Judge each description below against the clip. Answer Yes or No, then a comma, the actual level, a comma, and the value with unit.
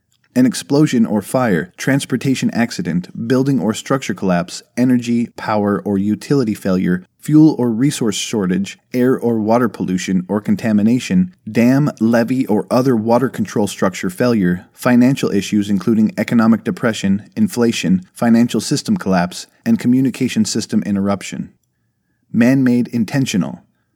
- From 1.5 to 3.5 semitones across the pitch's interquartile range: No, average, 4.1 semitones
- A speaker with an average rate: No, slow, 125 wpm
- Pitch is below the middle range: Yes, low, 120 Hz